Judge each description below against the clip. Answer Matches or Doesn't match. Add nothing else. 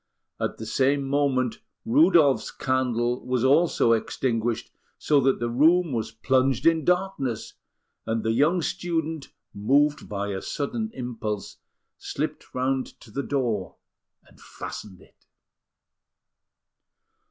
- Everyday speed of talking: Doesn't match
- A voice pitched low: Matches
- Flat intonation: Doesn't match